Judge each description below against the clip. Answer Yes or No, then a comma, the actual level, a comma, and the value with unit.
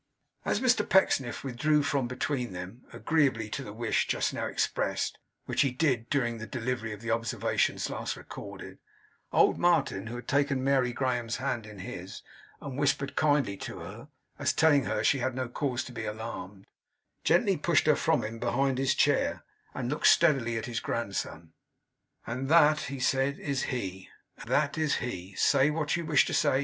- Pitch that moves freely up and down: No, average, 3.8 semitones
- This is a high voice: No, low, 125 Hz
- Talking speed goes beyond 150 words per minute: Yes, average, 180 wpm